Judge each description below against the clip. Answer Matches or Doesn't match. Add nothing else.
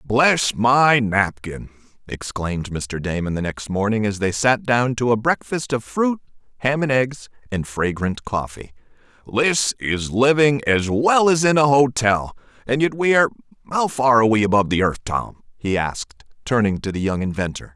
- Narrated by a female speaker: Doesn't match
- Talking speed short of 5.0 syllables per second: Matches